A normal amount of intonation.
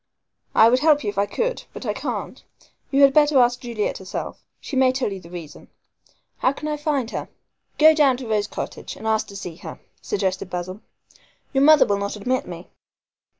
No: wide, 5.9 semitones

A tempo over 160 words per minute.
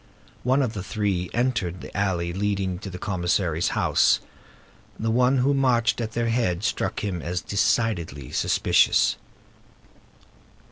No: slow, 135 wpm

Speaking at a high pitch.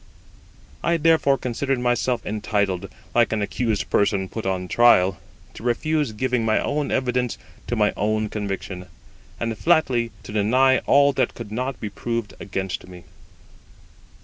No: low, 115 Hz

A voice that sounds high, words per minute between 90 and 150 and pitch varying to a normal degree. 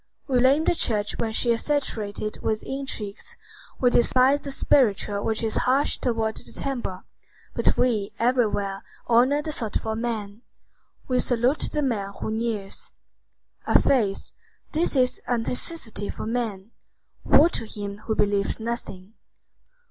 Yes: high, 230 Hz; average, 140 wpm; average, 3.6 semitones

